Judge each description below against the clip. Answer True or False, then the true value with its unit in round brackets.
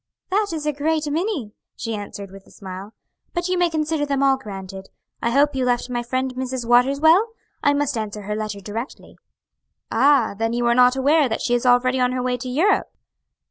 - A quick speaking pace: True (210 wpm)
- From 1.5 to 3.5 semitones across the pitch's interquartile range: False (4.5 semitones)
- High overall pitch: True (255 Hz)